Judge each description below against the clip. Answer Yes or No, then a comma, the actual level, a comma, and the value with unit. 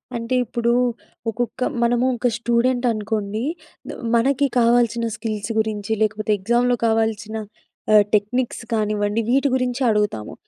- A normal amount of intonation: No, narrow, 2.3 semitones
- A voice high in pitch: Yes, high, 230 Hz